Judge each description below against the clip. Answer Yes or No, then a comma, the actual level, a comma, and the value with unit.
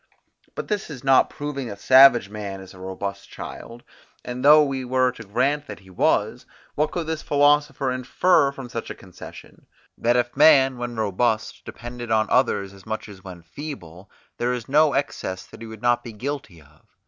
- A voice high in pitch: No, low, 120 Hz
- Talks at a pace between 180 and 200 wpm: Yes, average, 195 wpm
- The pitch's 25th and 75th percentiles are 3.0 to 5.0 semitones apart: No, wide, 5.4 semitones